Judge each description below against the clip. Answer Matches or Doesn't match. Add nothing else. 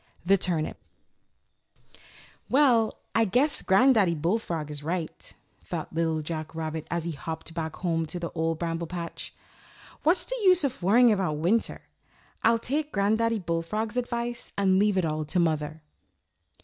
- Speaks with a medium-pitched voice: Matches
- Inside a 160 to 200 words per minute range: Doesn't match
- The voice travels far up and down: Matches